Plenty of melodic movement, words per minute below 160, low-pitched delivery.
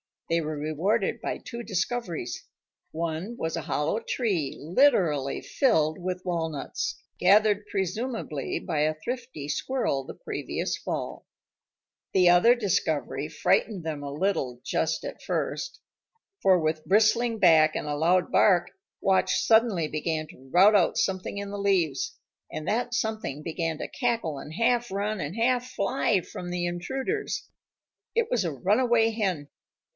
No: wide, 6.0 semitones; average, 145 wpm; medium, 180 Hz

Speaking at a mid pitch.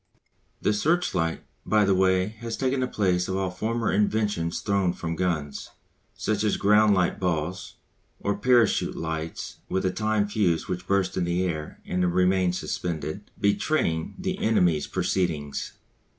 No: very low, 95 Hz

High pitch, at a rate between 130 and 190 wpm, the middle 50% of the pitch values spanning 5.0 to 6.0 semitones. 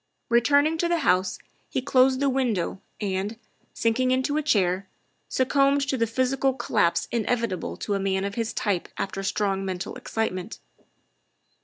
Yes: high, 230 Hz; average, 145 wpm; wide, 5.4 semitones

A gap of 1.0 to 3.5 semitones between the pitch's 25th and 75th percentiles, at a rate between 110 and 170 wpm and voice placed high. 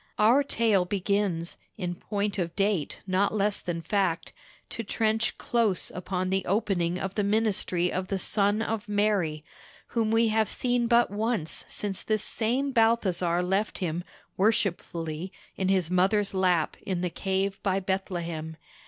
Yes: average, 3.2 semitones; average, 150 wpm; high, 195 Hz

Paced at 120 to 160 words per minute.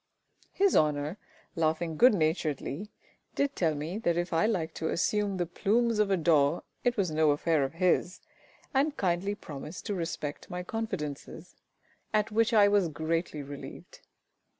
Yes: average, 155 wpm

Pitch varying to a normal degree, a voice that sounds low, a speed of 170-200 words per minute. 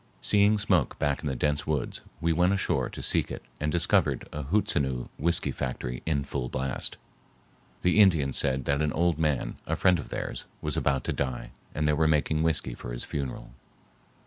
Yes: average, 3.6 semitones; very low, 75 Hz; average, 190 wpm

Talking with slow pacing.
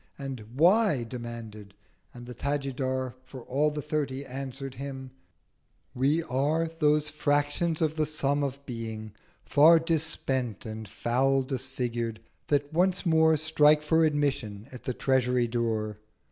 Yes: slow, 130 wpm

